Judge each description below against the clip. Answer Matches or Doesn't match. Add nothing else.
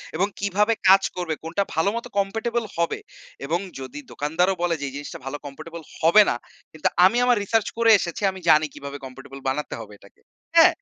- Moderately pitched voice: Matches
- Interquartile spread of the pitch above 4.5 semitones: Matches